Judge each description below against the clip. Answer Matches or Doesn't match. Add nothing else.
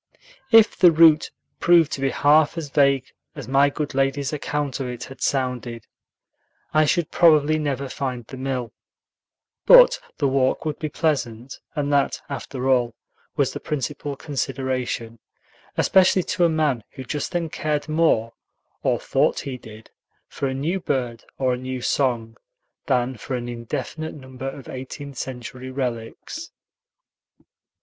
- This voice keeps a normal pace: Matches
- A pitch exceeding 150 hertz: Doesn't match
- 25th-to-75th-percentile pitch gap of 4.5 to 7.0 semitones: Doesn't match